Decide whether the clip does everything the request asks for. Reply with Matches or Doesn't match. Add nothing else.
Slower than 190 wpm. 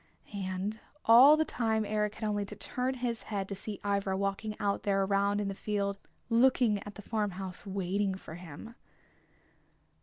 Matches